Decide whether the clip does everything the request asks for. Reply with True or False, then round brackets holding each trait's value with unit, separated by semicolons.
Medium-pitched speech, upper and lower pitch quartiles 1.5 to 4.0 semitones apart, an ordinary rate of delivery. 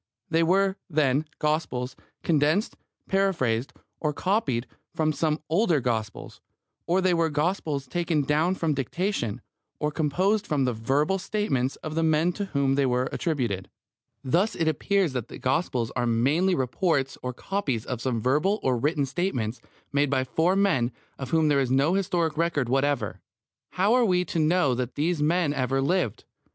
False (150 Hz; 5.2 semitones; 165 wpm)